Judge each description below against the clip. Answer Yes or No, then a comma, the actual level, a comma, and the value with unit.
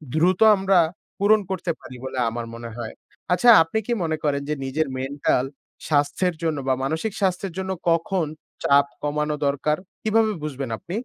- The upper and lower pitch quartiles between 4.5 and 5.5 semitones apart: Yes, average, 5.2 semitones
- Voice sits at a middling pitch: Yes, medium, 160 Hz